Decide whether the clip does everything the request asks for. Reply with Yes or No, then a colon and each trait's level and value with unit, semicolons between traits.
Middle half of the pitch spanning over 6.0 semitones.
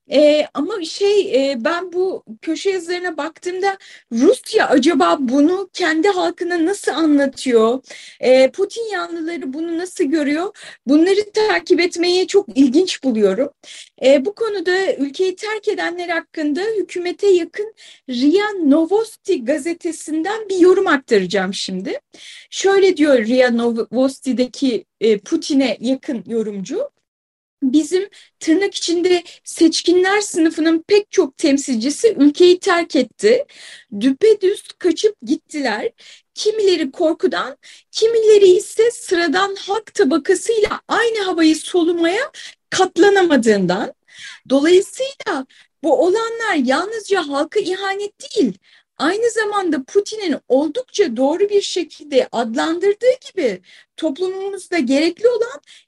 No: wide, 5.5 semitones